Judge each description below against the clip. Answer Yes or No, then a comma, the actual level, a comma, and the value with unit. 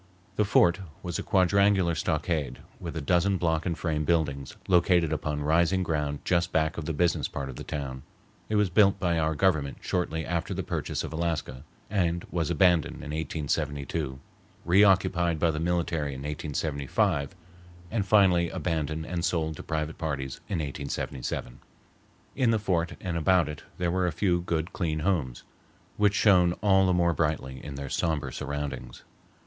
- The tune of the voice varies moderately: Yes, average, 3.1 semitones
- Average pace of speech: Yes, average, 165 wpm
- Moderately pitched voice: No, very low, 85 Hz